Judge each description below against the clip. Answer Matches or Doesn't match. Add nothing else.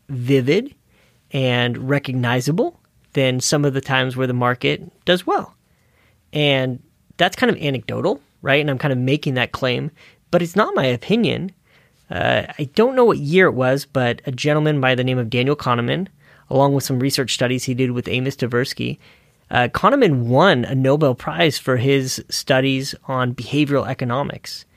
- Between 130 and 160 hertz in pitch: Matches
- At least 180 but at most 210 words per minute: Doesn't match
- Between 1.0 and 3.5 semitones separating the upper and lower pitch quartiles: Matches